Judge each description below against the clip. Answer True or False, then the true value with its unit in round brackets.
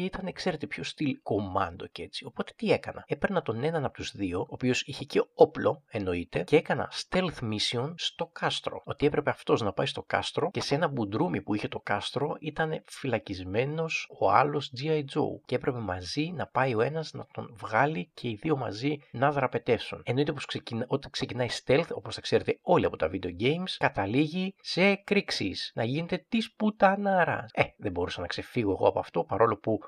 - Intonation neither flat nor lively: False (6.4 semitones)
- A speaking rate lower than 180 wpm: False (195 wpm)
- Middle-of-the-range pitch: True (145 Hz)